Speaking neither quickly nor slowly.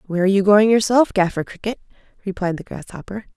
Yes: average, 180 wpm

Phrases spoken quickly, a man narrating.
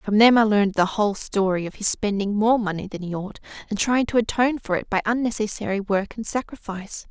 No: fast, 220 wpm; female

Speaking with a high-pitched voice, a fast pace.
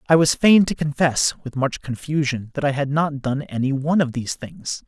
No: medium, 140 Hz; fast, 220 wpm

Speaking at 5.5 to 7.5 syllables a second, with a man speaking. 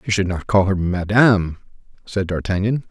No: 5.2 syllables/s; male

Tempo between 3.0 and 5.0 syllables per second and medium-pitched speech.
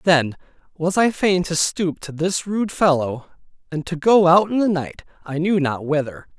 Yes: 4.5 syllables/s; medium, 170 Hz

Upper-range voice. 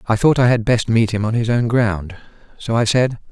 No: low, 115 Hz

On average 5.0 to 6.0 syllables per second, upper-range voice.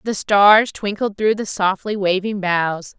No: 3.8 syllables/s; high, 200 Hz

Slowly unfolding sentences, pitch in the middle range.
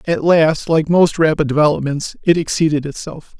Yes: slow, 125 wpm; medium, 155 Hz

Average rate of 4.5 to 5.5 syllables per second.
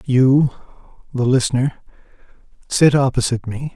Yes: 5.0 syllables/s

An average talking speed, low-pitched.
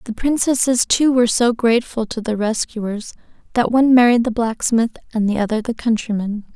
No: average, 175 wpm; high, 230 Hz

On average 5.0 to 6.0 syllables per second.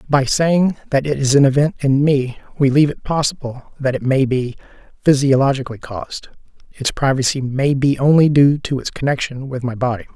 Yes: 5.5 syllables/s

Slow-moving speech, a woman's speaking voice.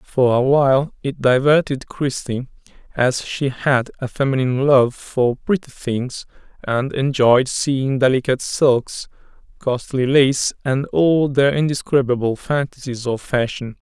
No: slow, 125 wpm; male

